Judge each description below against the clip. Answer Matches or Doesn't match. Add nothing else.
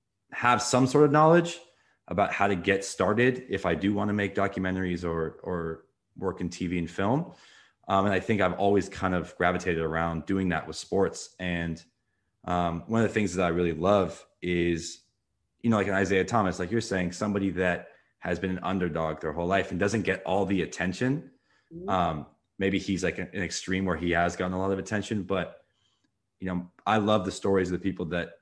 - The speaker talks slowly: Doesn't match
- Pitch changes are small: Matches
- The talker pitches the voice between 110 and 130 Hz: Doesn't match